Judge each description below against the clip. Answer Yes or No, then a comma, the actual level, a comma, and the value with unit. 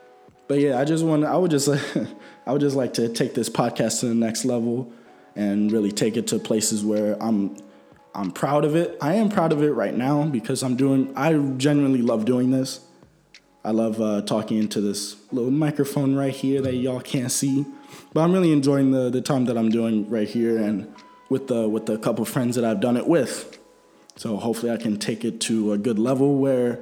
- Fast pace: Yes, fast, 210 wpm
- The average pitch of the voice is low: Yes, low, 125 Hz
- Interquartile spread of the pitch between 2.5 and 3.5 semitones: No, average, 3.9 semitones